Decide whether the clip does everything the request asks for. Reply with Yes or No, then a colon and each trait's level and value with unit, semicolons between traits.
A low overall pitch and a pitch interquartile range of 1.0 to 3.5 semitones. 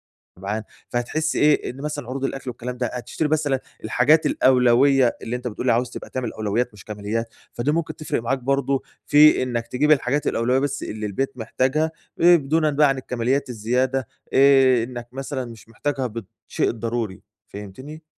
Yes: low, 130 Hz; average, 3.1 semitones